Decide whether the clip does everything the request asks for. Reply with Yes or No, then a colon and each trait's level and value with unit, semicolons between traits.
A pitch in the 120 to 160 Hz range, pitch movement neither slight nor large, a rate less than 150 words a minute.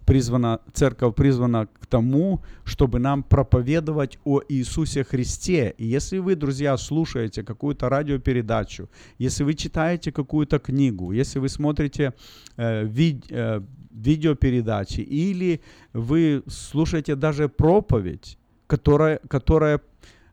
Yes: medium, 140 Hz; average, 4.0 semitones; slow, 110 wpm